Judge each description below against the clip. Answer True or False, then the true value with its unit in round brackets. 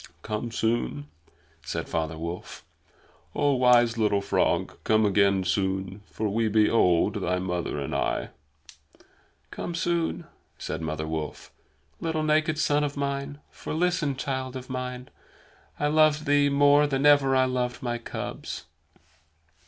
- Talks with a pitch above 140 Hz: False (125 Hz)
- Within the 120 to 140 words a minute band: True (135 wpm)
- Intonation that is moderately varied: False (6.4 semitones)